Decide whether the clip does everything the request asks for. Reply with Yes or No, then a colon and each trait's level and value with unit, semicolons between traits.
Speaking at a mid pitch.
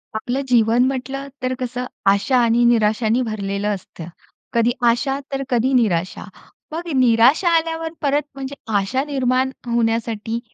No: high, 245 Hz